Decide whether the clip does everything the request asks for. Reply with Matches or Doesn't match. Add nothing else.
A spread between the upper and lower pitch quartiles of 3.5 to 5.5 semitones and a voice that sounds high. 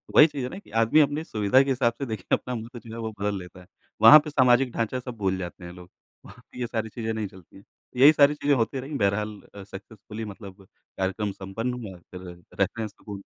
Doesn't match